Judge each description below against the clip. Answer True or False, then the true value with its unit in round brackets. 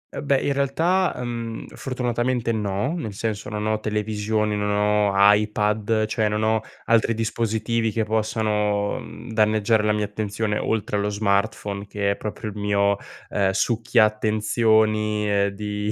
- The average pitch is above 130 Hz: False (110 Hz)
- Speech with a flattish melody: True (1.4 semitones)